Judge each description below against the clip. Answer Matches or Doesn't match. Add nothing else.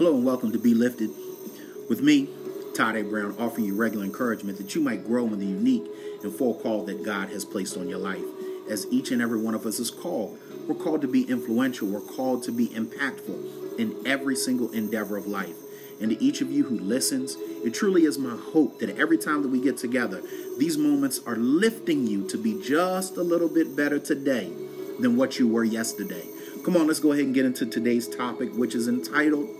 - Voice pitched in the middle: Matches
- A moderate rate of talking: Doesn't match